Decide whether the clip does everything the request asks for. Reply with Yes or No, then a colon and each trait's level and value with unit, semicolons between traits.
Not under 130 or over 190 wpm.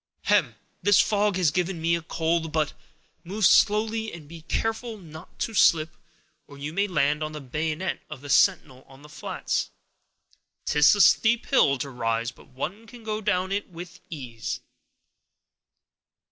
Yes: average, 155 wpm